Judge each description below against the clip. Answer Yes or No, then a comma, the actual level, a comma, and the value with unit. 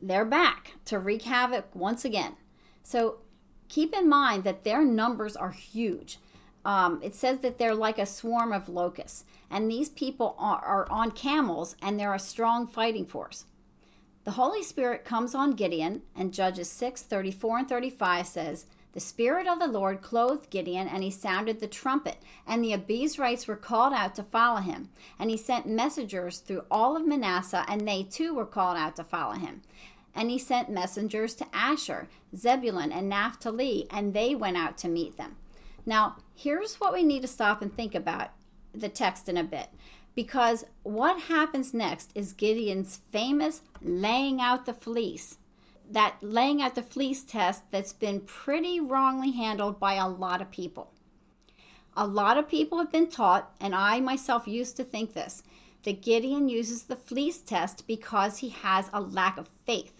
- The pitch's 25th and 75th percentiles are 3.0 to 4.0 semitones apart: No, average, 4.6 semitones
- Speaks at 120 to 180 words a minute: Yes, average, 175 wpm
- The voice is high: Yes, high, 225 Hz